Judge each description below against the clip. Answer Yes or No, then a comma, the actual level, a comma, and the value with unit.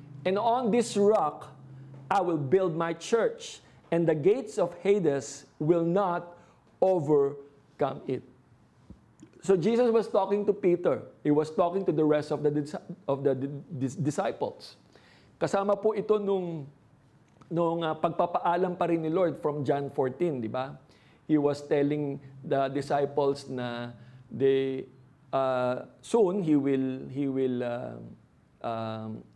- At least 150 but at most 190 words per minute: No, average, 135 wpm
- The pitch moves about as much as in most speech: Yes, average, 4.8 semitones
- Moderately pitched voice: Yes, medium, 150 Hz